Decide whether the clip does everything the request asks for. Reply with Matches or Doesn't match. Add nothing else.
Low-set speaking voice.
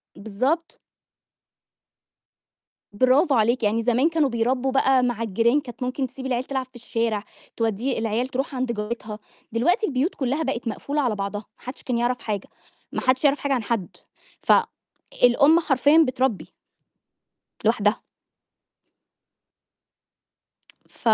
Doesn't match